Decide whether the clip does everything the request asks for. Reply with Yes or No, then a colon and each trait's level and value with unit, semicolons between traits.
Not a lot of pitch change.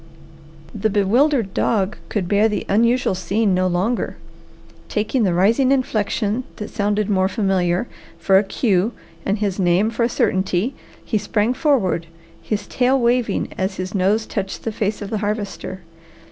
No: average, 3.0 semitones